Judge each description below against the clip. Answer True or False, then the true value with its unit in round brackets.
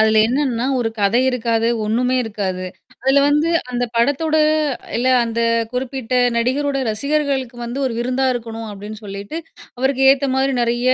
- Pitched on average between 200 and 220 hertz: False (245 Hz)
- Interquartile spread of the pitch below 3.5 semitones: True (3.0 semitones)